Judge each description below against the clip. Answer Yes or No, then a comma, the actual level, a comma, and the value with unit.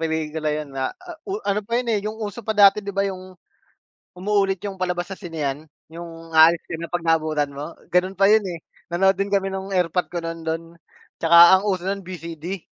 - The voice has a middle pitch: Yes, medium, 180 Hz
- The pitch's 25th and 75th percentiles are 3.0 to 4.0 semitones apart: Yes, average, 3.3 semitones